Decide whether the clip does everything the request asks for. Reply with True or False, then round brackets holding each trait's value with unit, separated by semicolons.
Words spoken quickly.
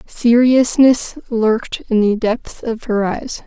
False (140 wpm)